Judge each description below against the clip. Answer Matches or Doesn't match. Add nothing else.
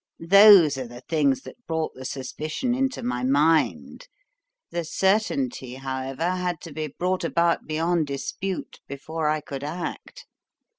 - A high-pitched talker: Doesn't match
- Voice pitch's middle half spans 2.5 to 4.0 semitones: Doesn't match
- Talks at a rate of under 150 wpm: Matches